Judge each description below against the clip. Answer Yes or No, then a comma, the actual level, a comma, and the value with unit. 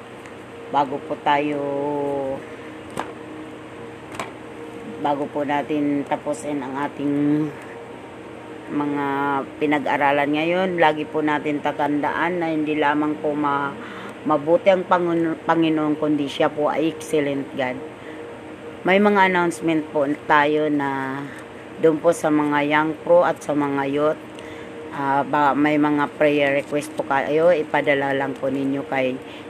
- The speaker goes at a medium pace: Yes, average, 120 wpm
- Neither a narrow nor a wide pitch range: No, narrow, 1.4 semitones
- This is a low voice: No, medium, 150 Hz